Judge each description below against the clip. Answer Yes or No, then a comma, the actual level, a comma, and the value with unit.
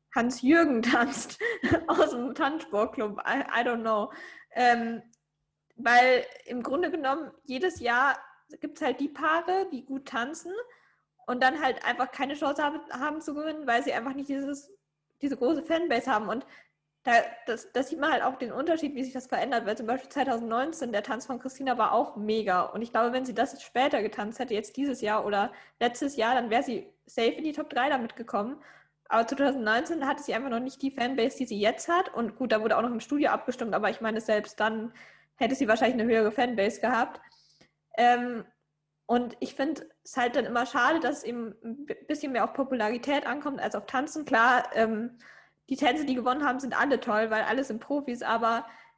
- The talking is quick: Yes, fast, 195 wpm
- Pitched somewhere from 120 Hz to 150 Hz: No, high, 245 Hz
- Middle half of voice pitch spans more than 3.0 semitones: Yes, average, 3.4 semitones